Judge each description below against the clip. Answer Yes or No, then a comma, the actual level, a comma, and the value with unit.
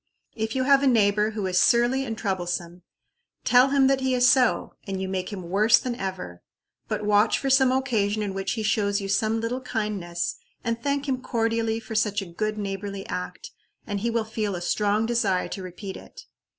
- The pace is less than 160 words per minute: No, fast, 205 wpm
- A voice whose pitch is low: No, high, 215 Hz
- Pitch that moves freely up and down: No, average, 3.6 semitones